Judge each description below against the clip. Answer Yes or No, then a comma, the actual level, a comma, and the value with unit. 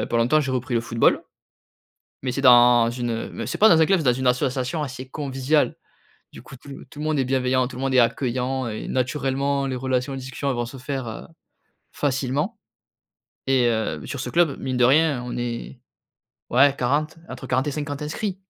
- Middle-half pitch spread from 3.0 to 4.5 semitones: No, narrow, 2.4 semitones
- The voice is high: No, low, 130 Hz